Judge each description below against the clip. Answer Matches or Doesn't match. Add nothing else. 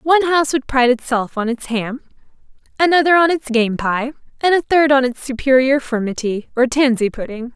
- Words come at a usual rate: Matches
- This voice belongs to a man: Doesn't match